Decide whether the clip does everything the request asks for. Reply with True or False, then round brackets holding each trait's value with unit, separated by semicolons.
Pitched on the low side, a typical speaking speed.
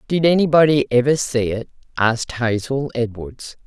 False (130 Hz; 130 wpm)